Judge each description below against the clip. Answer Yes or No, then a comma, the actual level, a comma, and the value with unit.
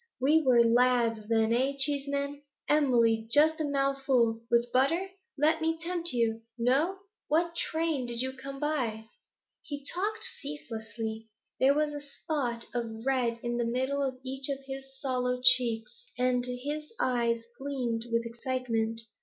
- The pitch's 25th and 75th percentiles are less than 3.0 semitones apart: No, average, 3.5 semitones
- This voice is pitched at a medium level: No, very high, 260 Hz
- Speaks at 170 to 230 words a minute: No, average, 145 wpm